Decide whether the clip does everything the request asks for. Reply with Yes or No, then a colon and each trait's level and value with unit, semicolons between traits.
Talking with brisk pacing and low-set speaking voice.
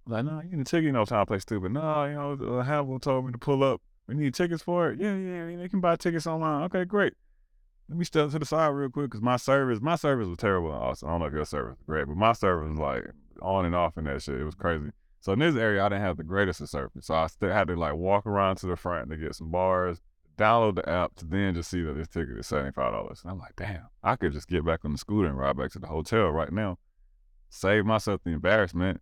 Yes: fast, 285 wpm; low, 100 Hz